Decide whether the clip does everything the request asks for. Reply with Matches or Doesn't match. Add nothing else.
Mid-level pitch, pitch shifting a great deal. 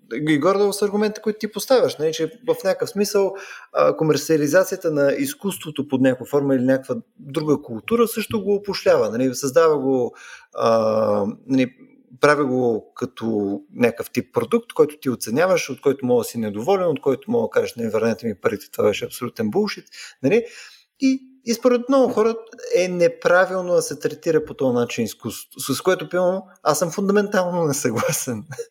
Matches